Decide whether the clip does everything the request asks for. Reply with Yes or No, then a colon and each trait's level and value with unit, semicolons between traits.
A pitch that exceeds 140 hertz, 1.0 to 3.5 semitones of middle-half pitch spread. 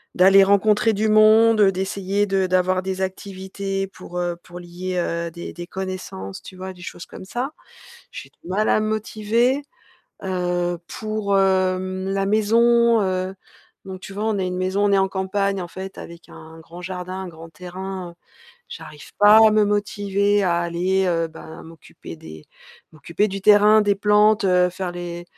Yes: high, 190 Hz; narrow, 2.4 semitones